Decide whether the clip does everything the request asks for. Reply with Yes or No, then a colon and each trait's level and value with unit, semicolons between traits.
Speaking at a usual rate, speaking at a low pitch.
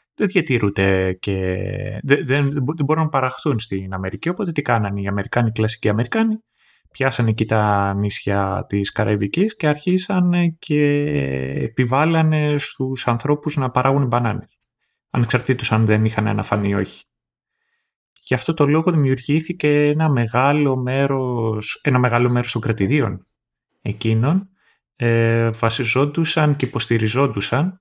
Yes: average, 125 wpm; low, 130 Hz